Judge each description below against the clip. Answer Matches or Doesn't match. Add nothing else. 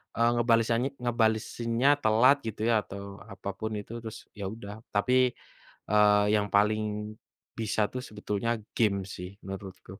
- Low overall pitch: Matches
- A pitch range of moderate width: Doesn't match